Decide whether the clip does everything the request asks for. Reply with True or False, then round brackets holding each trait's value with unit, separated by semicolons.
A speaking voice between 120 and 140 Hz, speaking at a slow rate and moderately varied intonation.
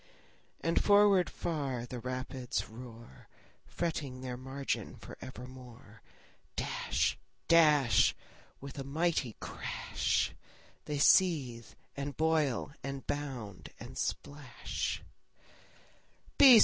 True (135 Hz; 90 wpm; 3.5 semitones)